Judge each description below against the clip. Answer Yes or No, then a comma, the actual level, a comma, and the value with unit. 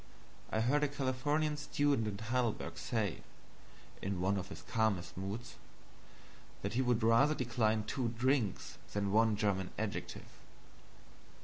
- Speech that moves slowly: Yes, slow, 130 wpm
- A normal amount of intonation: Yes, average, 4.0 semitones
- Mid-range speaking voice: No, low, 115 Hz